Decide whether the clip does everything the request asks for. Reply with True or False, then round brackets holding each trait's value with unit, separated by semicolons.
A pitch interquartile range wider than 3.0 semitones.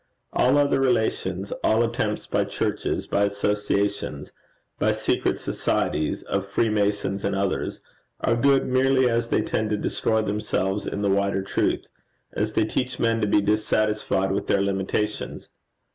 False (2.6 semitones)